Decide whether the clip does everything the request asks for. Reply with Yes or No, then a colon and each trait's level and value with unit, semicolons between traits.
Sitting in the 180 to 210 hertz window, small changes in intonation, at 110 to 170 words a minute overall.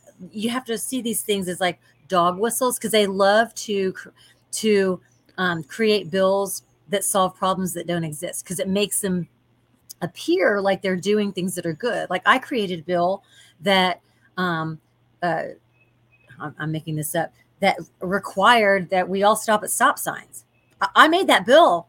No: medium, 185 Hz; average, 4.0 semitones; average, 165 wpm